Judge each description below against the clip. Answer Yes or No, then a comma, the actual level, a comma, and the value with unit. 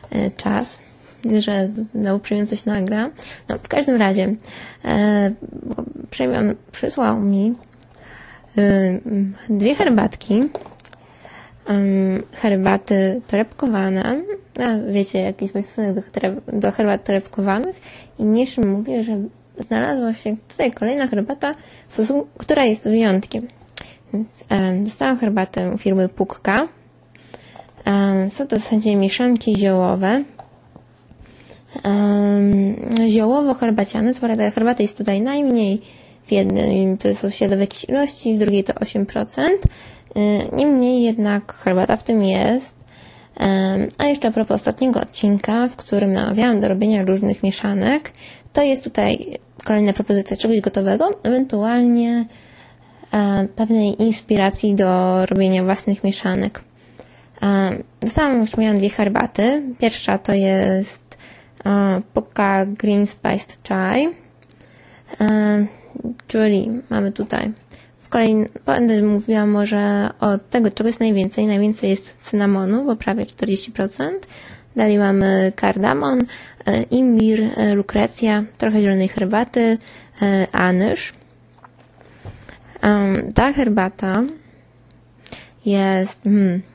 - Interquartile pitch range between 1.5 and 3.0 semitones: Yes, average, 2.7 semitones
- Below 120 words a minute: Yes, slow, 110 wpm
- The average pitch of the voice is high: Yes, high, 210 Hz